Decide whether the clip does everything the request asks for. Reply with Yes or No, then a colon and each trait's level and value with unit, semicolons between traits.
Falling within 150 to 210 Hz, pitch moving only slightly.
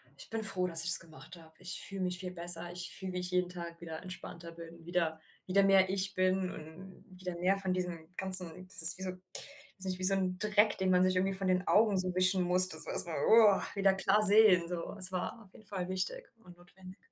Yes: medium, 185 Hz; narrow, 1.5 semitones